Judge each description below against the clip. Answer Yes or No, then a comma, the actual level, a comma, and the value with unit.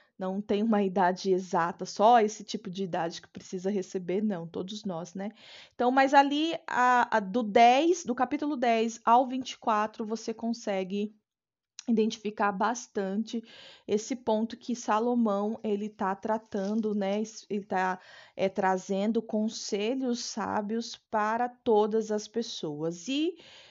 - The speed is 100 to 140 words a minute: Yes, average, 130 wpm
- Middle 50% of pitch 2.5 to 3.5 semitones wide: Yes, average, 2.9 semitones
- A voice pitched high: Yes, high, 215 Hz